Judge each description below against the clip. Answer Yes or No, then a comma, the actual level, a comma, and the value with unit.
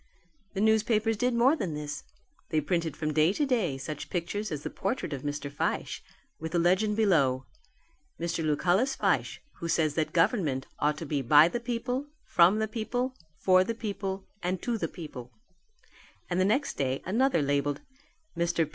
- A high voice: No, medium, 175 Hz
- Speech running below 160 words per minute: No, average, 175 wpm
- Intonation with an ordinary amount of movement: No, wide, 6.3 semitones